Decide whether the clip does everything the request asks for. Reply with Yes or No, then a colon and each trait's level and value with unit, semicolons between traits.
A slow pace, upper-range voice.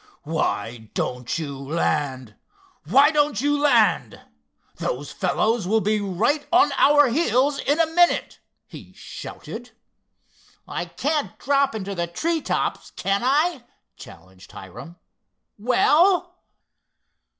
Yes: slow, 105 wpm; high, 235 Hz